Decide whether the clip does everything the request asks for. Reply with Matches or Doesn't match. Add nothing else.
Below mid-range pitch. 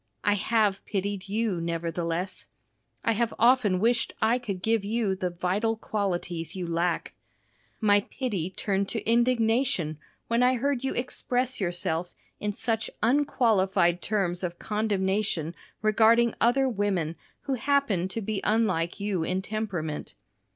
Doesn't match